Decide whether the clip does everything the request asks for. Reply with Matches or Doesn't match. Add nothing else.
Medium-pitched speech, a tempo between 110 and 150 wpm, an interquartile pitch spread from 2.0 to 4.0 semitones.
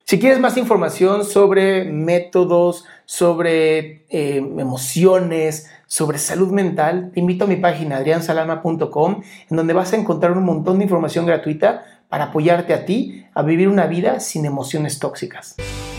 Matches